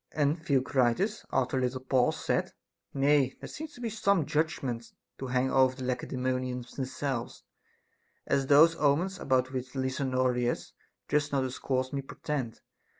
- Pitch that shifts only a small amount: Yes, narrow, 2.3 semitones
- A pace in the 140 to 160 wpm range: Yes, average, 145 wpm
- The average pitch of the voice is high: No, low, 130 Hz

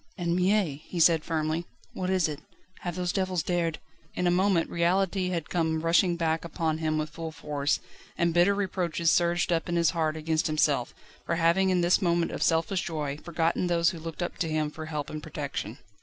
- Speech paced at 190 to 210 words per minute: Yes, fast, 205 wpm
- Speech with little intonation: Yes, narrow, 2.0 semitones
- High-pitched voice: No, medium, 170 Hz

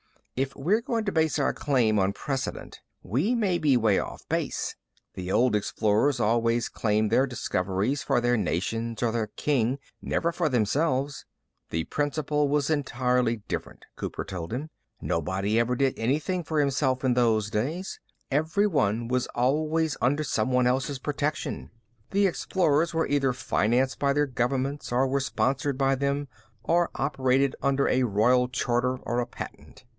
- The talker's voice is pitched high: No, low, 130 Hz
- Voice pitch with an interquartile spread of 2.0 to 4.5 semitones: Yes, average, 3.8 semitones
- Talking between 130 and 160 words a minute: Yes, average, 155 wpm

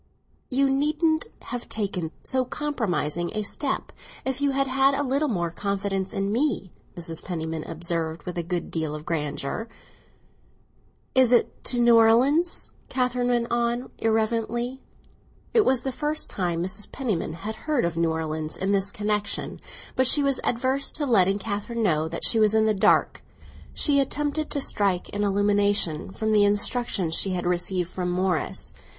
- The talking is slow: No, average, 165 wpm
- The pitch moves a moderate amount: No, wide, 6.4 semitones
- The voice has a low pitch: No, high, 215 Hz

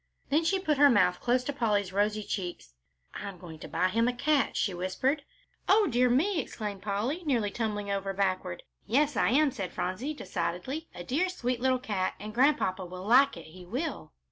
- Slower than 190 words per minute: No, average, 195 wpm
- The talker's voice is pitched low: No, high, 225 Hz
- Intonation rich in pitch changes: Yes, wide, 6.6 semitones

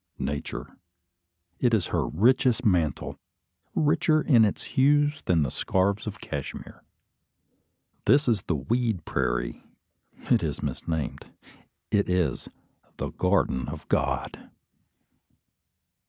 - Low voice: Yes, low, 100 Hz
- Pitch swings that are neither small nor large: No, wide, 7.9 semitones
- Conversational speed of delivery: No, slow, 110 wpm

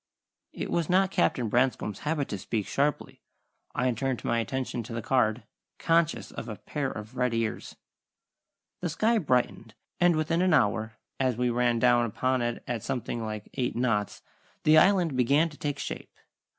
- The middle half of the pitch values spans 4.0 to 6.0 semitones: Yes, average, 4.5 semitones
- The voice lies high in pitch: No, low, 125 Hz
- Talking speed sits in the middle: Yes, average, 170 wpm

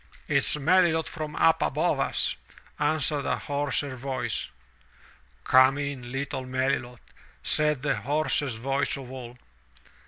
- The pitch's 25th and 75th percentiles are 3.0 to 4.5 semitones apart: No, narrow, 2.5 semitones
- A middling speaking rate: No, slow, 120 wpm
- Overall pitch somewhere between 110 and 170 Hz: Yes, medium, 140 Hz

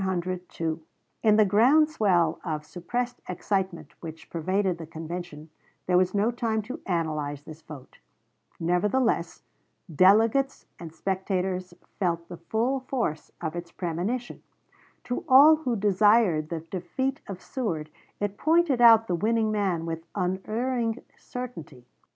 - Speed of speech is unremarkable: No, slow, 125 wpm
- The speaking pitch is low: No, high, 190 Hz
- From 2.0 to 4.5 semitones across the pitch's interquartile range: No, wide, 5.5 semitones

